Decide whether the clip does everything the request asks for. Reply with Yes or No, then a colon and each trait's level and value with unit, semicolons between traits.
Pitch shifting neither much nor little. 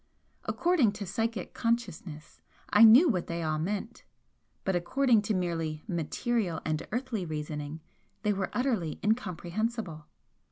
No: wide, 5.8 semitones